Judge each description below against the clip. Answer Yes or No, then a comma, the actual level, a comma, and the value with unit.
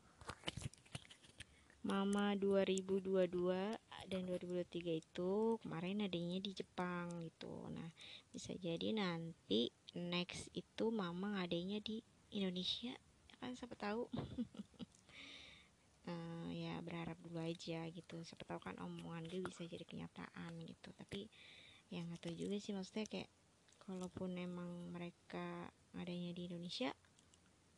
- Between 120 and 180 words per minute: No, average, 110 wpm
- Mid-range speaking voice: Yes, medium, 180 Hz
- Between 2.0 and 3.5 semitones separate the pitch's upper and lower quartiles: Yes, average, 2.8 semitones